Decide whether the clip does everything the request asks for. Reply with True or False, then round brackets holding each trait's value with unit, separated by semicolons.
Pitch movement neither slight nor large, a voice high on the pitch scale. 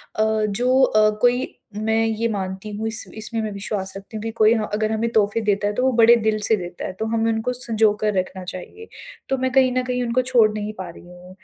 False (2.3 semitones; 220 Hz)